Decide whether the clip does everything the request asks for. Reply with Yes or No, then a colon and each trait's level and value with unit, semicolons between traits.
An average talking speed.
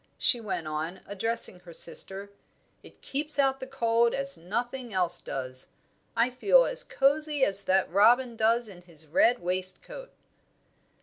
Yes: average, 145 wpm